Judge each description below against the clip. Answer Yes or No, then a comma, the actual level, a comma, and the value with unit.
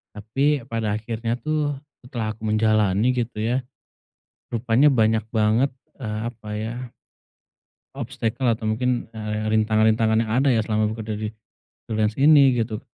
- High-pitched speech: No, low, 110 Hz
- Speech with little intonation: Yes, narrow, 1.9 semitones